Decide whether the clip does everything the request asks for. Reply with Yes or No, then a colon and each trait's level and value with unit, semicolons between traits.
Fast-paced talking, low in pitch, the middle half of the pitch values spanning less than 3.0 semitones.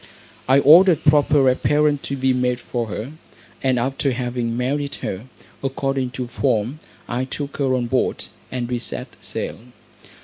No: average, 150 wpm; low, 130 Hz; narrow, 2.4 semitones